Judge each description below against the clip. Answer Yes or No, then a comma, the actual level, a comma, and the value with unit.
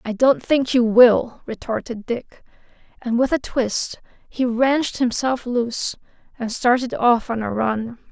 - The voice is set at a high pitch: Yes, high, 240 Hz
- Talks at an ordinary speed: Yes, average, 155 wpm